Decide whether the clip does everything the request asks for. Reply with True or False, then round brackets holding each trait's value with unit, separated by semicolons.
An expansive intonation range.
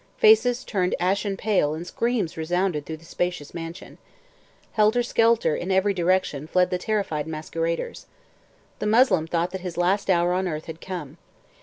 False (3.6 semitones)